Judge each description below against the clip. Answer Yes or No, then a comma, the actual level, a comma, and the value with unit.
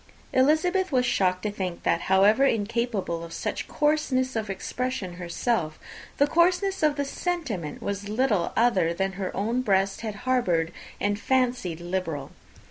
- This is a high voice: Yes, high, 215 Hz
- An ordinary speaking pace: Yes, average, 150 wpm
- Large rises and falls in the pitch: Yes, wide, 5.9 semitones